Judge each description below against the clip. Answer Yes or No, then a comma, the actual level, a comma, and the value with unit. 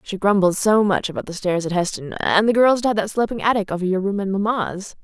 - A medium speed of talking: No, fast, 275 wpm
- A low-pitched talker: No, high, 200 Hz